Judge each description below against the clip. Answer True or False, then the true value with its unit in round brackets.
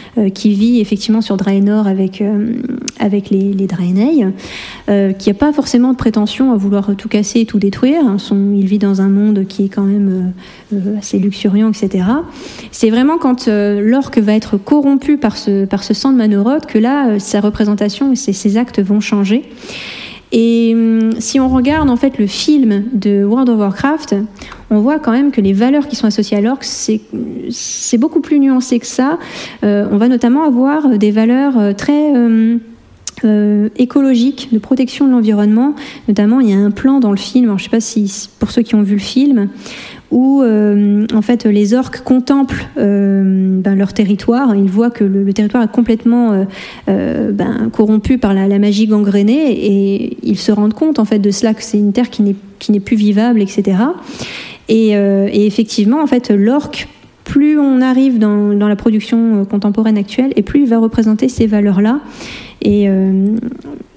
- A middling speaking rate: True (195 wpm)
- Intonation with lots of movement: False (3.7 semitones)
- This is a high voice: True (220 Hz)